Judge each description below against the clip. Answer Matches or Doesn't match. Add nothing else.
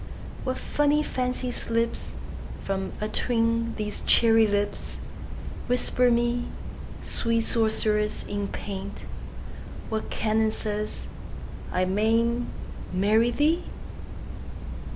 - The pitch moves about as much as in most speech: Doesn't match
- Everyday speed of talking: Doesn't match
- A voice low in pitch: Doesn't match